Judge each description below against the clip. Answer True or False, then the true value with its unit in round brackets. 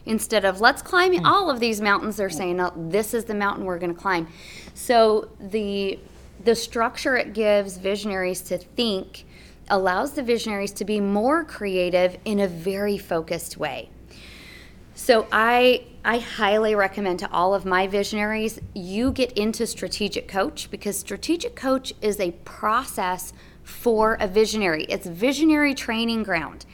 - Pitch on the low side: False (205 Hz)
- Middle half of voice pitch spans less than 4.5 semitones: True (3.6 semitones)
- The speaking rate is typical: True (150 wpm)